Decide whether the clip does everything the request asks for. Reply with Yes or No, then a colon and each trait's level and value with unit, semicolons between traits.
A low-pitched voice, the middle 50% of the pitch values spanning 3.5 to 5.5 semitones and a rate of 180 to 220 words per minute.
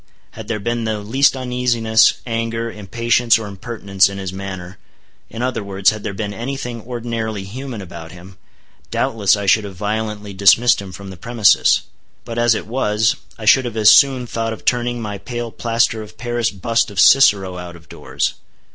No: low, 110 Hz; average, 3.1 semitones; average, 185 wpm